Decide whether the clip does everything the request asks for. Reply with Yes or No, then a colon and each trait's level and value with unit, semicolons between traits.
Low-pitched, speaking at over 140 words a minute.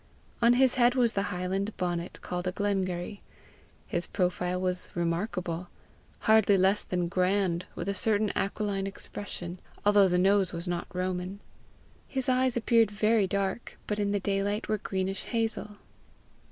No: high, 195 Hz; average, 150 wpm